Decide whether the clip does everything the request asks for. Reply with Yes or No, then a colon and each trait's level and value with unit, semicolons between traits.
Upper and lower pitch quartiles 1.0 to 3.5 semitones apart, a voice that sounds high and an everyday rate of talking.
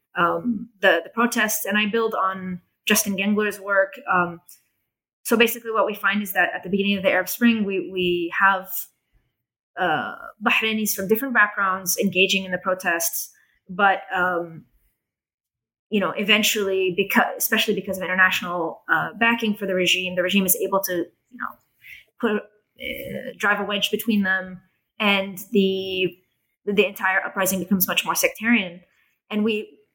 Yes: narrow, 2.6 semitones; high, 195 Hz; average, 155 wpm